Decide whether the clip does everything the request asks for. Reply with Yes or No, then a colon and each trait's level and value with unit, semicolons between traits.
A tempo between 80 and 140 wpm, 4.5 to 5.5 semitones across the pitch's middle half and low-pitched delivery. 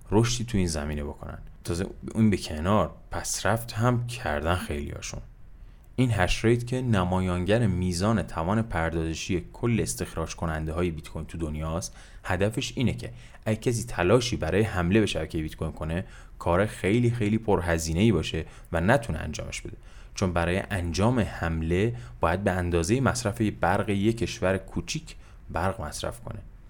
No: average, 150 wpm; average, 5.1 semitones; very low, 95 Hz